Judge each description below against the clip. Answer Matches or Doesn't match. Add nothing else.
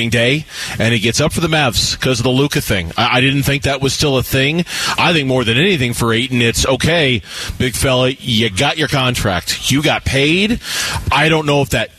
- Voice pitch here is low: Matches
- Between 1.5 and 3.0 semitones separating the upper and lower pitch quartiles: Doesn't match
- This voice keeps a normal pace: Doesn't match